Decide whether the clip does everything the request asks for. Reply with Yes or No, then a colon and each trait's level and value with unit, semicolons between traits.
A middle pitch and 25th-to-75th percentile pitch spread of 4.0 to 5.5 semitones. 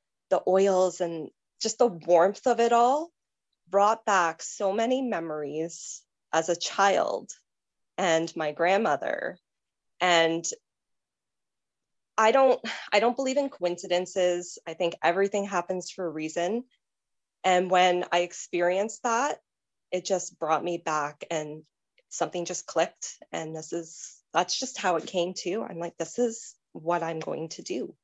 No: medium, 180 Hz; average, 3.4 semitones